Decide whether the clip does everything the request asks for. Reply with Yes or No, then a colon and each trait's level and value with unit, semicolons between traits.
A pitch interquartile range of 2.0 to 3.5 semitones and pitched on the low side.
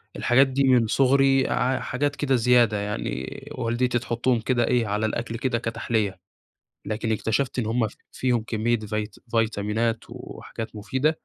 Yes: average, 2.7 semitones; low, 120 Hz